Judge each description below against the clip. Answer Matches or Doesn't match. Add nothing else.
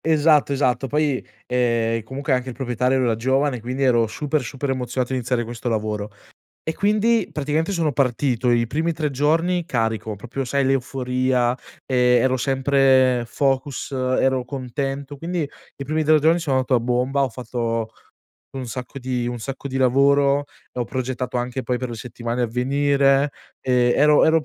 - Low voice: Matches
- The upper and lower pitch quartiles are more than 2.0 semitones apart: Matches